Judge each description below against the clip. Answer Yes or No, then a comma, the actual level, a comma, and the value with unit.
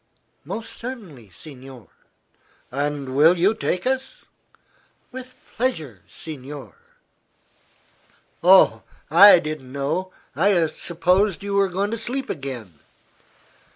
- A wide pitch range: Yes, wide, 6.5 semitones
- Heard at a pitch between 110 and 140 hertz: No, medium, 170 Hz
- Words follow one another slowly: Yes, slow, 100 wpm